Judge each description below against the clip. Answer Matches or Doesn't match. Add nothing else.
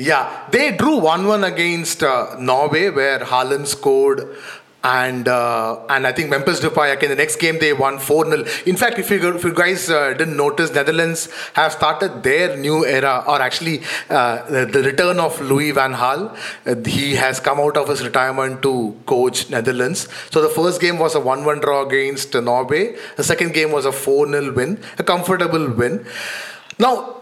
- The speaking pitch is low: Doesn't match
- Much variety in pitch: Doesn't match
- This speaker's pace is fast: Doesn't match